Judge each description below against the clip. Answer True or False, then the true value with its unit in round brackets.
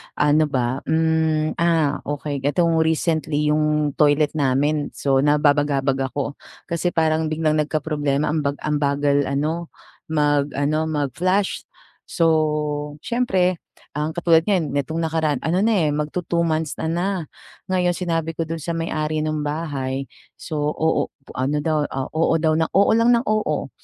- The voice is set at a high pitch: False (155 Hz)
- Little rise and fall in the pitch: True (2.0 semitones)